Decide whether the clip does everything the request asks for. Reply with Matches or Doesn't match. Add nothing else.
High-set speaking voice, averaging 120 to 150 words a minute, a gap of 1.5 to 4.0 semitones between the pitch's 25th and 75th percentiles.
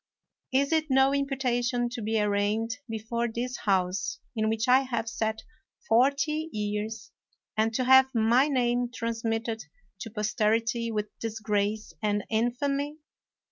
Matches